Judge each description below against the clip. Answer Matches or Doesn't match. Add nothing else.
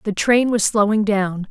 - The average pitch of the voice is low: Doesn't match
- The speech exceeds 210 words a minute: Doesn't match